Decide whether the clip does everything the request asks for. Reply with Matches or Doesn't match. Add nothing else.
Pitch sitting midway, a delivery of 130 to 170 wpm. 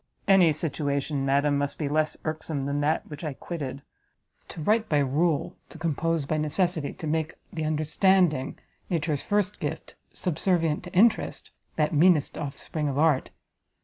Matches